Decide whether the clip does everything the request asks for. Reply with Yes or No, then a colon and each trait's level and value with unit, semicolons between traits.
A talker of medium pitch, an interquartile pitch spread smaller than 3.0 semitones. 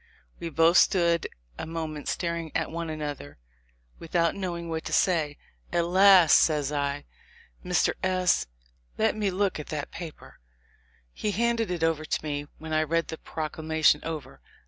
Yes: medium, 165 Hz; narrow, 2.4 semitones